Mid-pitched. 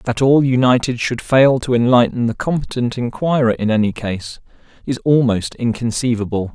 No: low, 120 Hz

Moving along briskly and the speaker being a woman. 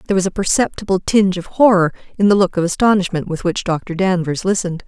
Yes: fast, 210 wpm; female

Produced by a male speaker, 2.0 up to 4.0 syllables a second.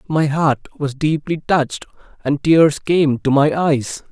Yes: male; 3.9 syllables/s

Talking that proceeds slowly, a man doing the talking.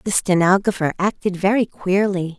No: slow, 125 wpm; female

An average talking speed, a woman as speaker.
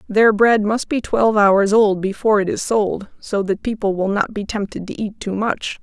No: fast, 225 wpm; female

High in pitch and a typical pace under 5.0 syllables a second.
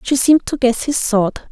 No: very high, 255 Hz; 5.3 syllables/s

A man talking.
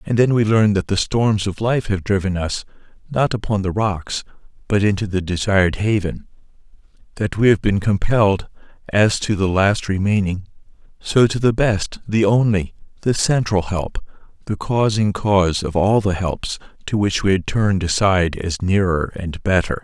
Yes: male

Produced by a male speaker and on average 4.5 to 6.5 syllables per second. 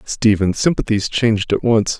Yes: male; 4.8 syllables/s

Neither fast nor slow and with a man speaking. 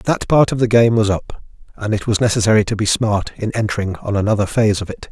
No: fast, 235 wpm; male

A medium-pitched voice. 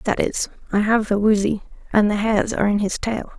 No: high, 210 Hz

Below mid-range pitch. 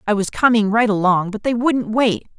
No: high, 220 Hz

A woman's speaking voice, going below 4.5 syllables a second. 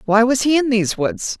No: female; 5.6 syllables/s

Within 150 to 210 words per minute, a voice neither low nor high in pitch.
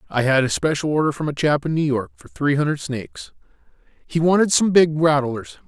Yes: average, 200 wpm; medium, 150 Hz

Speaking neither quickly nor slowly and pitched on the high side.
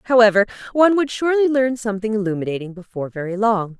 Yes: average, 160 wpm; high, 220 Hz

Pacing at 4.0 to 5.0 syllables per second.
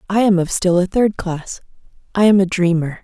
No: 5.2 syllables/s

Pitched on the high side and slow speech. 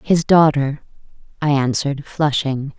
No: medium, 145 Hz; slow, 110 wpm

